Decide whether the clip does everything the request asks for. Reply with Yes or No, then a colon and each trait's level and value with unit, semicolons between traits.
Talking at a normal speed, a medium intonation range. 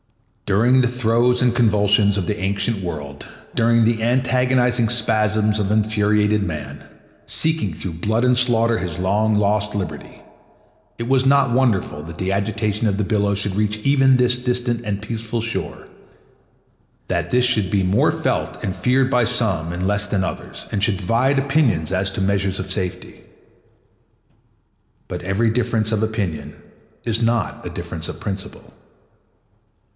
Yes: average, 155 wpm; average, 3.5 semitones